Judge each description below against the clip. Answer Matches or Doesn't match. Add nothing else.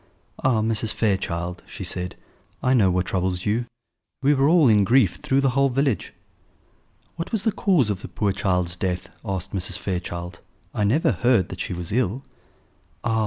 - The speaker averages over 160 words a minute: Matches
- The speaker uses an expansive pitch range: Matches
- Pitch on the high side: Doesn't match